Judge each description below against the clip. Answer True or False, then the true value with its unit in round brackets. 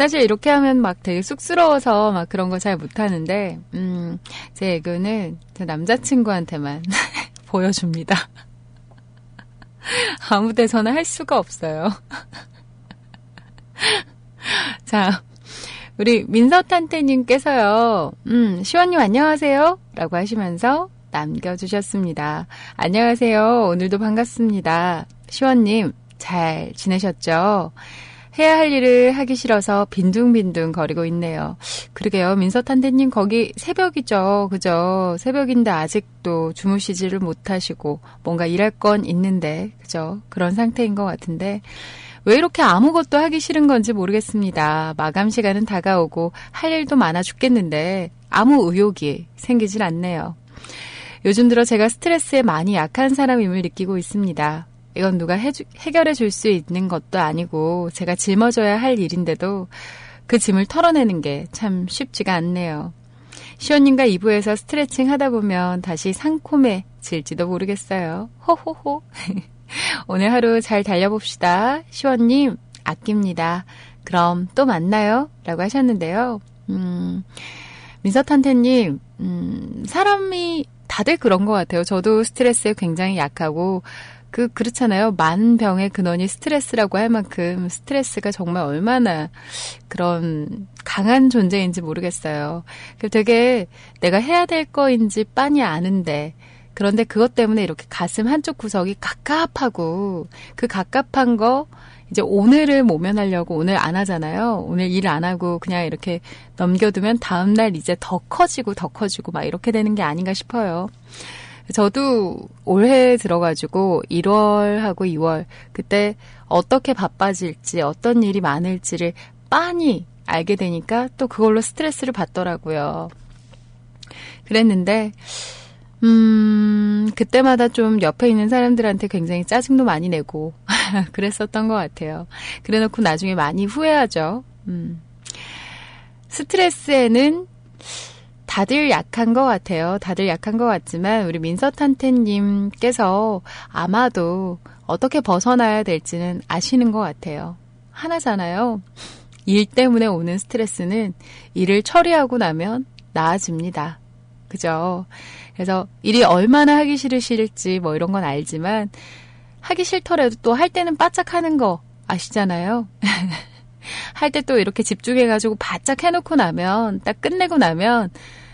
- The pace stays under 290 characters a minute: True (280 characters per minute)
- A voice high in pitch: True (200 Hz)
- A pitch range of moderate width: False (5.7 semitones)